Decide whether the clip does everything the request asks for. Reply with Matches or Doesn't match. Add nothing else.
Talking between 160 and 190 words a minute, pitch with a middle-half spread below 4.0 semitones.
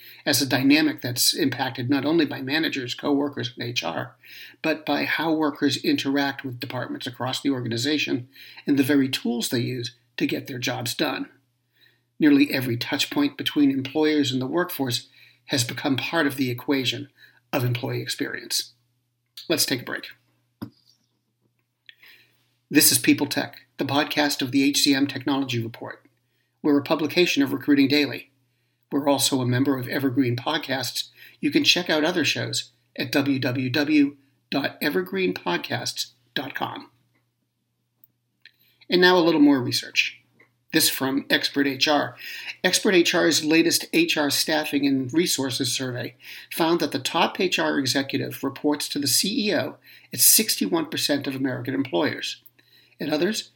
Doesn't match